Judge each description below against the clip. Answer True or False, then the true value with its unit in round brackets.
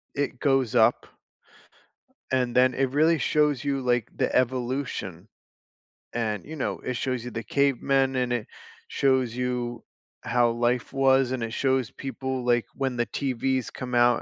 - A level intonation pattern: True (1.8 semitones)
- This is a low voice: True (125 Hz)